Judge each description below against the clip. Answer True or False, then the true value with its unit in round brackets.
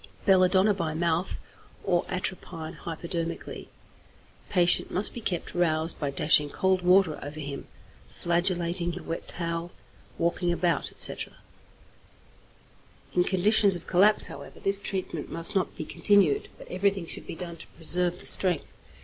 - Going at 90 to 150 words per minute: True (140 wpm)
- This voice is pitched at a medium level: True (175 Hz)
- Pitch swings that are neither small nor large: False (2.2 semitones)